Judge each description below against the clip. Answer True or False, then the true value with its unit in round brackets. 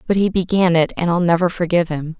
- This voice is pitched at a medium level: True (175 Hz)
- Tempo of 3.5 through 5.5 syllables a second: False (6.3 syllables/s)